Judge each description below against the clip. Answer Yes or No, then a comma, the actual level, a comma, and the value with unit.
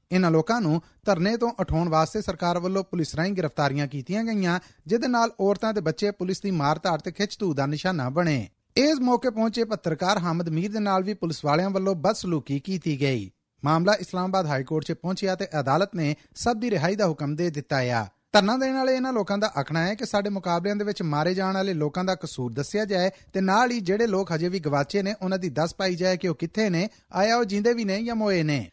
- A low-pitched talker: No, medium, 185 Hz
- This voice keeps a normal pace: No, fast, 220 wpm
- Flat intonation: No, average, 4.5 semitones